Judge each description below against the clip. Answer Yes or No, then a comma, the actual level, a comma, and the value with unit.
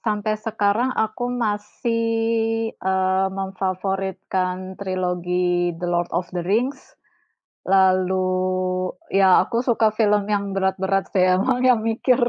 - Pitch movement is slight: No, average, 3.2 semitones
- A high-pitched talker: Yes, high, 195 Hz